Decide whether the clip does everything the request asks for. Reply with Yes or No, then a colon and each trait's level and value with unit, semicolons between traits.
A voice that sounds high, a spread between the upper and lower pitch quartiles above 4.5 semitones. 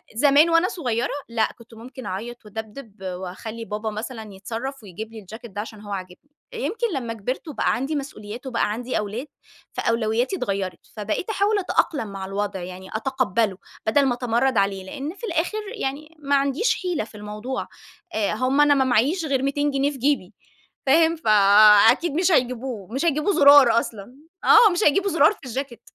Yes: high, 245 Hz; average, 5.2 semitones